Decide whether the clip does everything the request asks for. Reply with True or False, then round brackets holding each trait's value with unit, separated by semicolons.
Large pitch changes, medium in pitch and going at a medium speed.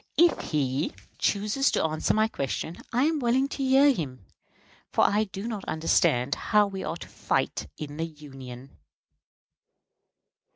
True (8.2 semitones; 180 Hz; 150 wpm)